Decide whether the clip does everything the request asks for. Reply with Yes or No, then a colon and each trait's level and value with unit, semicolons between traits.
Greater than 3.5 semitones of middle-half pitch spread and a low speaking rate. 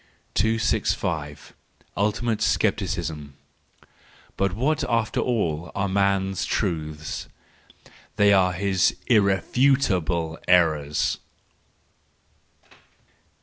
Yes: average, 4.5 semitones; slow, 65 wpm